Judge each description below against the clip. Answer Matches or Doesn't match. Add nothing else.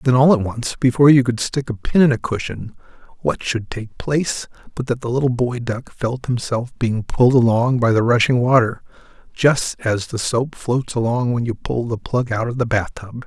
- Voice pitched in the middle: Doesn't match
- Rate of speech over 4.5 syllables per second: Matches